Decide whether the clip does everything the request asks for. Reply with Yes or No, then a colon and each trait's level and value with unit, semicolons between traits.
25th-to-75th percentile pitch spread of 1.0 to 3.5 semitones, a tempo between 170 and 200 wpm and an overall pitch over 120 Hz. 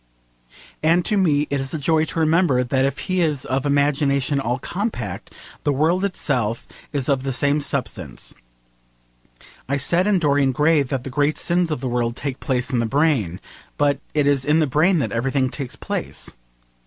Yes: average, 3.2 semitones; average, 185 wpm; medium, 140 Hz